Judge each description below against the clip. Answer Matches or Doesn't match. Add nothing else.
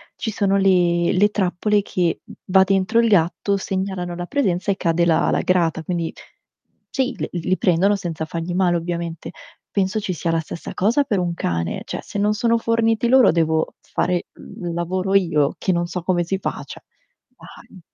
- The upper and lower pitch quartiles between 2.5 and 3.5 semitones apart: Matches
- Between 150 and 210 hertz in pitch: Matches